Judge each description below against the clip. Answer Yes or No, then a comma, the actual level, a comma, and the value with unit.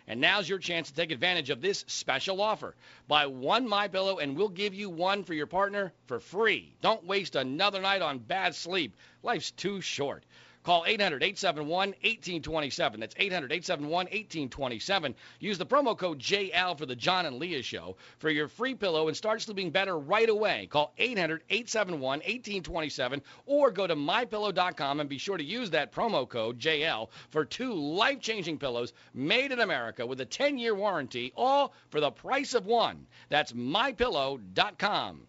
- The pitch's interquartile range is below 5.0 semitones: No, wide, 5.6 semitones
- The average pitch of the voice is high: No, medium, 180 Hz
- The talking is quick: No, average, 160 wpm